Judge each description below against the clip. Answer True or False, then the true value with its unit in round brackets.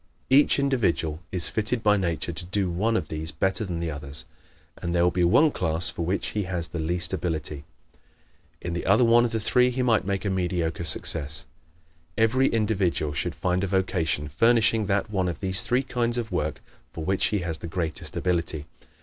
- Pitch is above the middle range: False (90 Hz)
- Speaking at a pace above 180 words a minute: True (200 wpm)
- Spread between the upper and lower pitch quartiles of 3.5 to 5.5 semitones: True (4.7 semitones)